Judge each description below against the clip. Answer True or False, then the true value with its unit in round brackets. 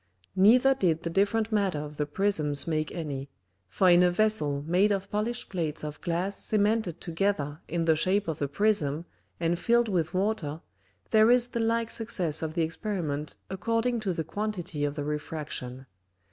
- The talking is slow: False (175 wpm)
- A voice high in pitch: False (175 Hz)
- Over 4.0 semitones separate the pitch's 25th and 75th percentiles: True (5.6 semitones)